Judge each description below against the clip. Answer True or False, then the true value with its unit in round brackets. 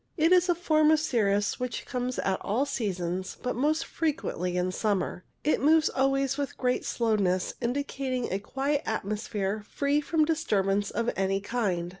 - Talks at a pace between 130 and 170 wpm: True (160 wpm)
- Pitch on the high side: True (245 Hz)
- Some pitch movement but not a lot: False (6.5 semitones)